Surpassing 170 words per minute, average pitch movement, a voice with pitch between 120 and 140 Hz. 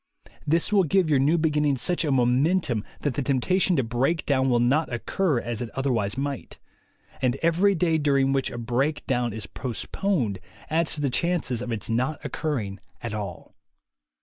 Yes: average, 180 wpm; average, 4.8 semitones; low, 135 Hz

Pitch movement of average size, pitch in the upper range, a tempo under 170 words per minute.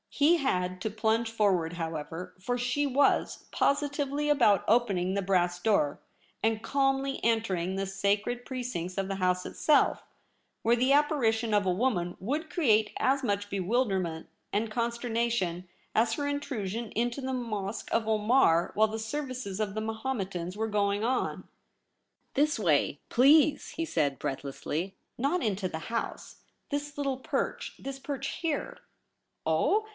No: wide, 5.7 semitones; high, 220 Hz; average, 150 wpm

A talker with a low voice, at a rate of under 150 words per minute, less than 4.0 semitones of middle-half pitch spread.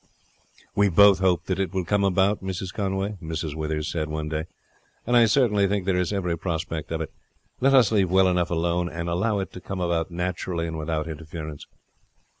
No: very low, 90 Hz; average, 195 wpm; average, 3.2 semitones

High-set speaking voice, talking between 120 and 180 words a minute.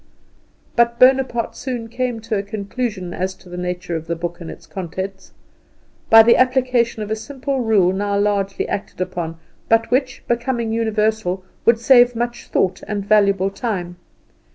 Yes: high, 215 Hz; average, 160 wpm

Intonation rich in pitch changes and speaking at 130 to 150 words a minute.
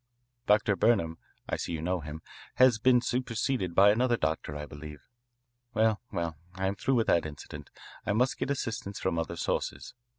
No: wide, 6.3 semitones; average, 175 wpm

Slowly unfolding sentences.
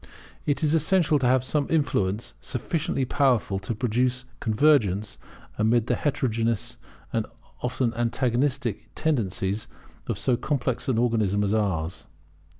Yes: slow, 125 wpm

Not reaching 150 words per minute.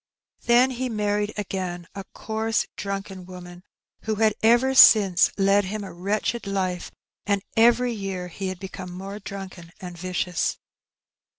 Yes: average, 140 wpm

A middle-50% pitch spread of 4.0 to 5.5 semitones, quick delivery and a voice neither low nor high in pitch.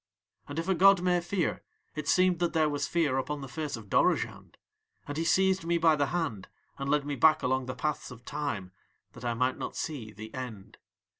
Yes: average, 4.7 semitones; fast, 215 wpm; medium, 150 Hz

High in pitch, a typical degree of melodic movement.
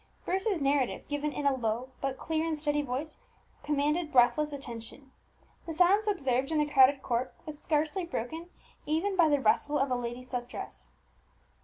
Yes: very high, 290 Hz; average, 3.6 semitones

